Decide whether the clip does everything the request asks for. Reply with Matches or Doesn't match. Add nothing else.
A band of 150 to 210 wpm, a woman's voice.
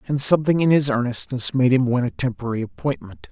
Doesn't match